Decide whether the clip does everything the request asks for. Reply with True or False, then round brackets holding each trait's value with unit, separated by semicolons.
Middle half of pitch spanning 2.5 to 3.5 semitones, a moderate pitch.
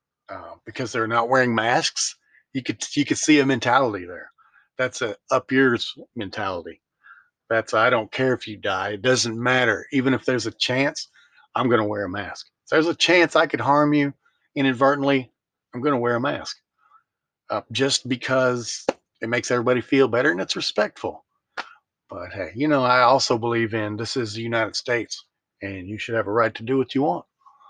False (2.8 semitones; 125 Hz)